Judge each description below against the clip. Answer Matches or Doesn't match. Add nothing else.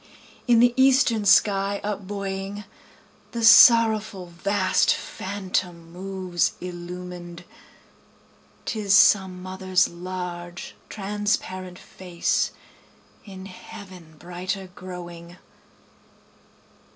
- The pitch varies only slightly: Matches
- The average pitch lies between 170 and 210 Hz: Matches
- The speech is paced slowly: Matches